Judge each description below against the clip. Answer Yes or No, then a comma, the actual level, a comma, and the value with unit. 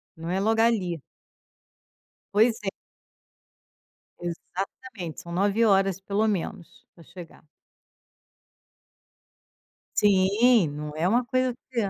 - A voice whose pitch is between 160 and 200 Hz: Yes, high, 195 Hz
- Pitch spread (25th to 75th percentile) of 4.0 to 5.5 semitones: Yes, average, 4.5 semitones